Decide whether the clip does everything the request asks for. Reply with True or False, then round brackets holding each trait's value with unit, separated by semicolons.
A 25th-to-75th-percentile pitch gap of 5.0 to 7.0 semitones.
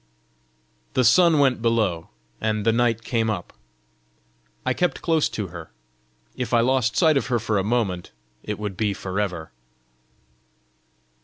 False (3.7 semitones)